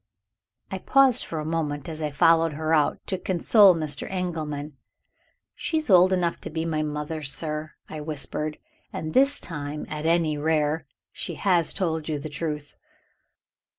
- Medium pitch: Yes, medium, 160 Hz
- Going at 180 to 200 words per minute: No, average, 160 wpm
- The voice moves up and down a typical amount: No, narrow, 2.3 semitones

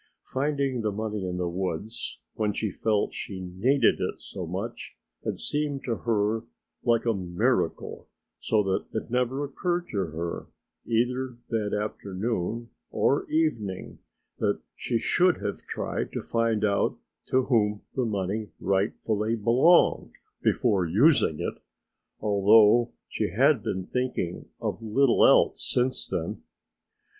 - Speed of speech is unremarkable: No, slow, 130 wpm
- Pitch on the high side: No, low, 110 Hz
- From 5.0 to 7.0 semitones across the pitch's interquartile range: No, average, 3.9 semitones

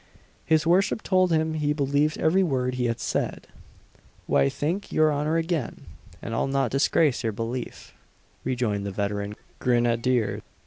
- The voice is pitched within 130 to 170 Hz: Yes, low, 135 Hz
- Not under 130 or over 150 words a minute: Yes, average, 145 wpm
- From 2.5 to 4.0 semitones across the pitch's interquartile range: No, average, 5.2 semitones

